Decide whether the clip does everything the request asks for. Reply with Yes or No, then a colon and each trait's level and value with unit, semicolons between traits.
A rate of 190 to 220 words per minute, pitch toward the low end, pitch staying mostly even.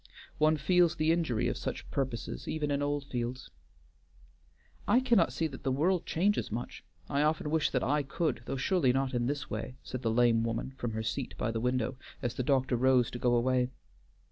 No: average, 195 wpm; low, 130 Hz; average, 4.0 semitones